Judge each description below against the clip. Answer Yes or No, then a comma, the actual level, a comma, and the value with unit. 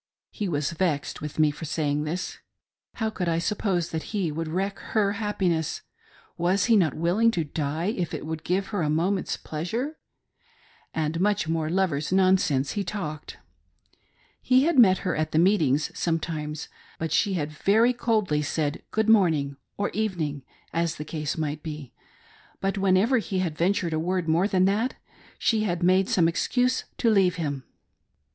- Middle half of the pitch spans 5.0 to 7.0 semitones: No, average, 4.4 semitones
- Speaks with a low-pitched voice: No, medium, 175 Hz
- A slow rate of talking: No, average, 180 wpm